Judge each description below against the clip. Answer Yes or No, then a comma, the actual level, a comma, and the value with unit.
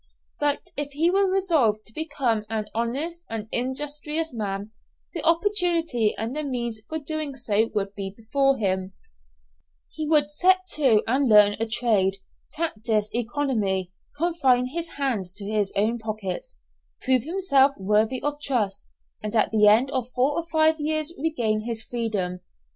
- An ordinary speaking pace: Yes, average, 155 wpm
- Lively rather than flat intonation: Yes, wide, 6.1 semitones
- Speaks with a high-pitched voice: Yes, very high, 250 Hz